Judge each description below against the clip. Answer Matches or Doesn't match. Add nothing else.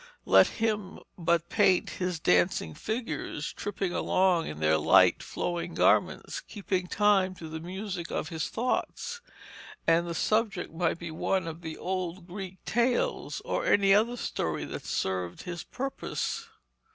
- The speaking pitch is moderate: Matches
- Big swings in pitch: Doesn't match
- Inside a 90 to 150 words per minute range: Matches